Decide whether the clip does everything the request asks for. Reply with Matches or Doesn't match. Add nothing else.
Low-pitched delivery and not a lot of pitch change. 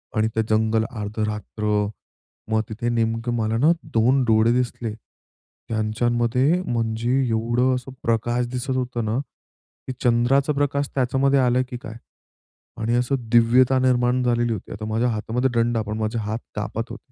Matches